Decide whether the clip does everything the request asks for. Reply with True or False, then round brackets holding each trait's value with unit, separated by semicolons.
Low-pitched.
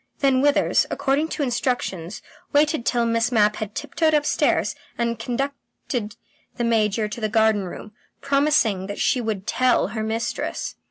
False (235 Hz)